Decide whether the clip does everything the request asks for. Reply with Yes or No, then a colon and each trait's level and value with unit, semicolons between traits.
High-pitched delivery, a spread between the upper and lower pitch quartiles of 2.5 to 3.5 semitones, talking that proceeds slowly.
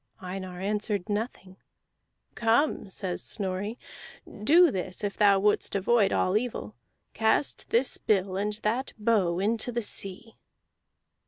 Yes: high, 205 Hz; average, 3.1 semitones; slow, 120 wpm